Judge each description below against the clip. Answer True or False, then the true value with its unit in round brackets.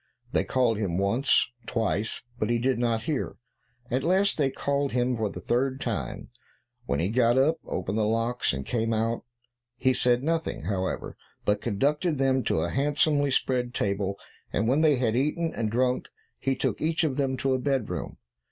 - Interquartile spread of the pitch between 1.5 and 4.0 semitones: True (3.6 semitones)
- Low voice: True (125 Hz)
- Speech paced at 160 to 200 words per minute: True (180 wpm)